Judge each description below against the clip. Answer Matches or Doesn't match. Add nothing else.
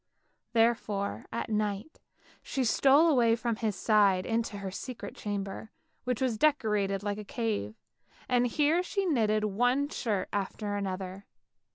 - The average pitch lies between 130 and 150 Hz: Doesn't match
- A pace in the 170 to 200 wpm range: Doesn't match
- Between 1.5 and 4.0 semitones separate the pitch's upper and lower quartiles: Matches